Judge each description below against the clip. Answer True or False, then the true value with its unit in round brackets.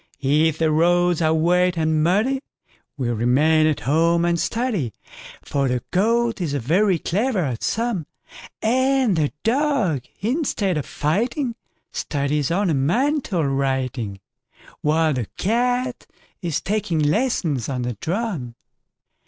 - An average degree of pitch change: False (7.3 semitones)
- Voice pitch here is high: False (170 Hz)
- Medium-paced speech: False (110 wpm)